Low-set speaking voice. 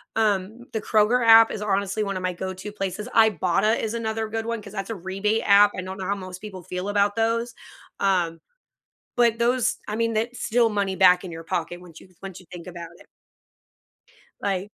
No: high, 205 Hz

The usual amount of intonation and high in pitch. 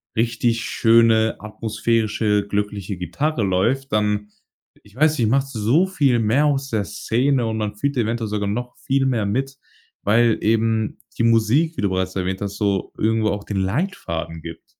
No: average, 3.2 semitones; low, 110 Hz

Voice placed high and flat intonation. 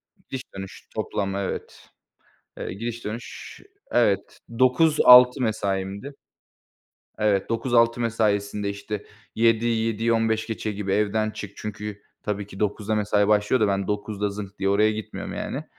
No: low, 105 Hz; narrow, 2.2 semitones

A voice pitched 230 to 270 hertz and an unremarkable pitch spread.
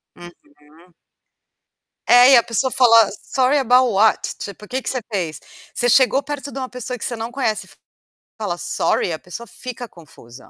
Yes: high, 235 Hz; average, 4.0 semitones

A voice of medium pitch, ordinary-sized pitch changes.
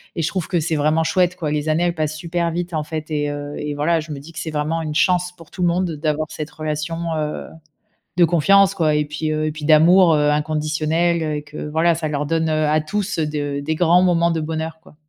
No: medium, 155 Hz; narrow, 2.0 semitones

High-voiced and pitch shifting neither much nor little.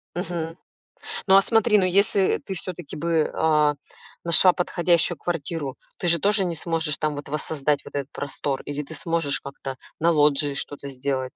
No: medium, 160 Hz; average, 3.5 semitones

